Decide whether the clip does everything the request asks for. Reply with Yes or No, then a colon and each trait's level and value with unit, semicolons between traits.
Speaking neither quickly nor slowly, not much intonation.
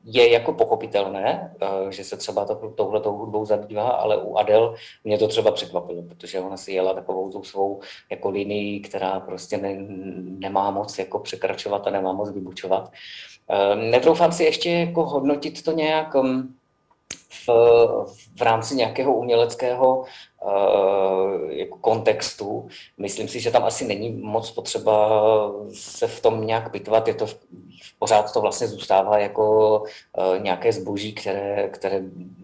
No: average, 140 wpm; average, 3.1 semitones